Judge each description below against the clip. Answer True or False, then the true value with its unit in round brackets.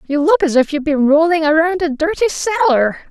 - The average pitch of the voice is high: True (320 Hz)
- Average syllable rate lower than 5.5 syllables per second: True (5.1 syllables/s)